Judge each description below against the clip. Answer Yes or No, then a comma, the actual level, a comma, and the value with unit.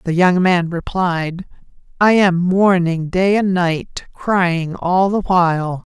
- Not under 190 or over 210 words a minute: No, average, 140 wpm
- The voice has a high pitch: No, medium, 180 Hz